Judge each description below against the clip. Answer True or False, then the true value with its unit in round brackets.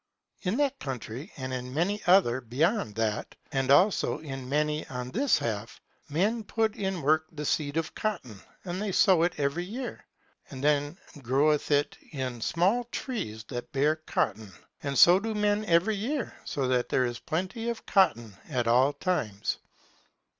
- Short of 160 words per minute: False (165 wpm)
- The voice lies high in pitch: False (150 Hz)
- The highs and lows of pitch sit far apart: True (7.2 semitones)